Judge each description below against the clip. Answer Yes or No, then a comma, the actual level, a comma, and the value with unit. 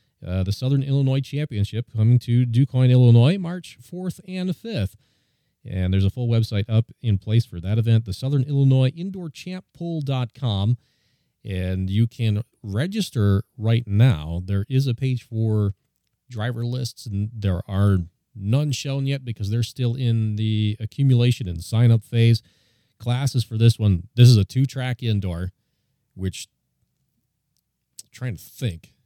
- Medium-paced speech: Yes, average, 150 wpm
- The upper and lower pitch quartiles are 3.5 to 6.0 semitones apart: Yes, average, 4.2 semitones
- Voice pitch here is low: Yes, low, 115 Hz